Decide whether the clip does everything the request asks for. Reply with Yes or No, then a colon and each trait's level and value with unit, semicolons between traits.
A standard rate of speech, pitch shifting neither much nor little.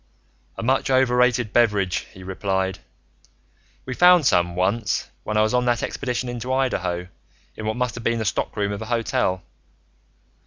Yes: average, 160 wpm; average, 4.3 semitones